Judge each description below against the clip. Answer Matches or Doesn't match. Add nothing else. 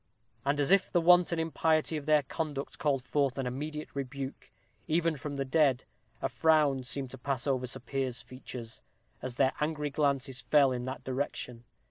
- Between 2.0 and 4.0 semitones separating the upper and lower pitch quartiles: Matches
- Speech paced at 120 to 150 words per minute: Doesn't match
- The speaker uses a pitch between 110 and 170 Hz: Matches